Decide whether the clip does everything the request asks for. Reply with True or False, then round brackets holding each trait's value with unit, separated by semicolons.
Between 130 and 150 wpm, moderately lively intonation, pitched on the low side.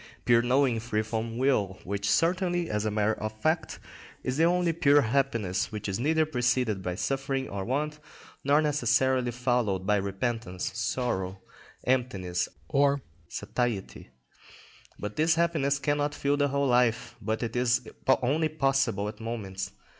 True (145 wpm; 5.0 semitones; 125 Hz)